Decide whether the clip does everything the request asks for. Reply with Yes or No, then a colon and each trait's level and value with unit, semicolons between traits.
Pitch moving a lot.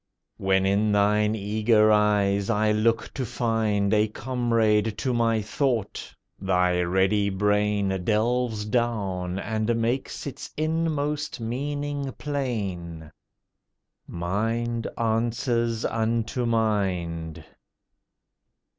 No: average, 2.8 semitones